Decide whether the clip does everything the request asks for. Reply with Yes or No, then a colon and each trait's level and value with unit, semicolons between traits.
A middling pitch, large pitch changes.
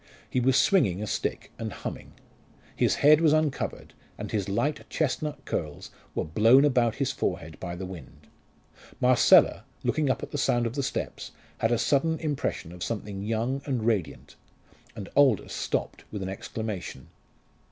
No: low, 115 Hz; wide, 6.1 semitones